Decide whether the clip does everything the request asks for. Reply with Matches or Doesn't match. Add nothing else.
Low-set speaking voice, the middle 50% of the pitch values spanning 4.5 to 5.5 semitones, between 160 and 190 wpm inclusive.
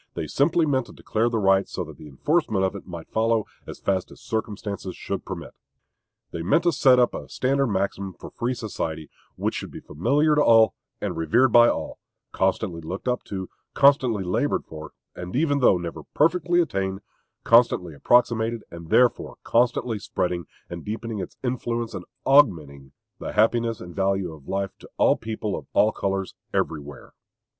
Matches